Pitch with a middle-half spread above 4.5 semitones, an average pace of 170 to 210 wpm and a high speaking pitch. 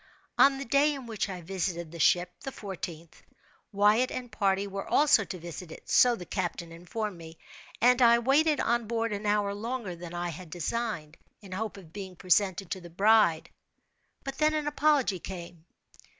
Yes: average, 5.2 semitones; average, 175 wpm; high, 200 Hz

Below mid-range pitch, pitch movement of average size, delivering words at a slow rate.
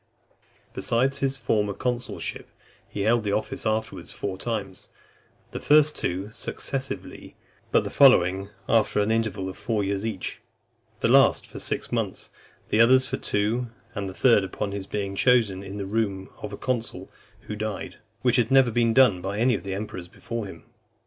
No: low, 110 Hz; average, 3.4 semitones; average, 175 wpm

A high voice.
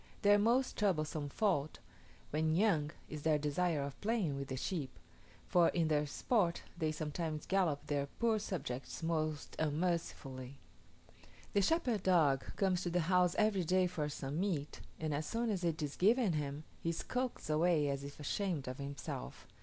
No: medium, 160 Hz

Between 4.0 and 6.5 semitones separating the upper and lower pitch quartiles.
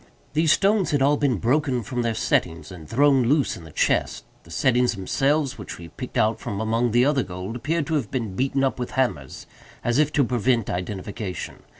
Yes: wide, 5.4 semitones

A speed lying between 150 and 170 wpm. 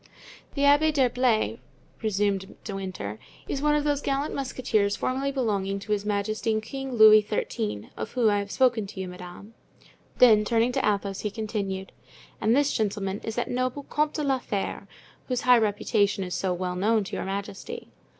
No: average, 180 wpm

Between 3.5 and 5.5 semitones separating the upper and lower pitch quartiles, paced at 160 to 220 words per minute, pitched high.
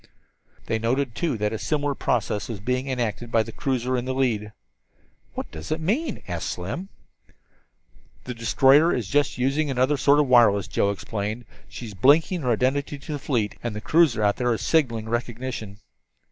No: average, 4.4 semitones; average, 180 wpm; low, 125 Hz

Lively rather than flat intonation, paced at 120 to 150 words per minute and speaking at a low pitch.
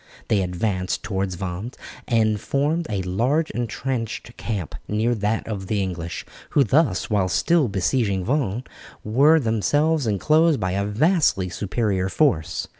Yes: wide, 6.0 semitones; slow, 135 wpm; low, 110 Hz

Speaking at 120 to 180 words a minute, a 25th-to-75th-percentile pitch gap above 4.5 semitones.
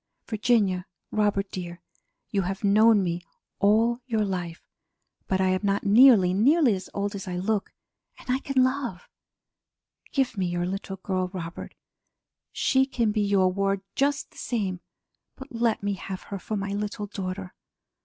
No: average, 160 wpm; average, 3.3 semitones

